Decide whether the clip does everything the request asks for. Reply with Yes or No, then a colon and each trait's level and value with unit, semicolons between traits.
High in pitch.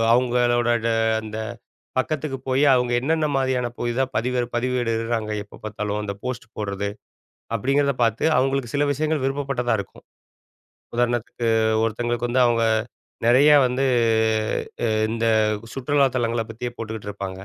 No: low, 120 Hz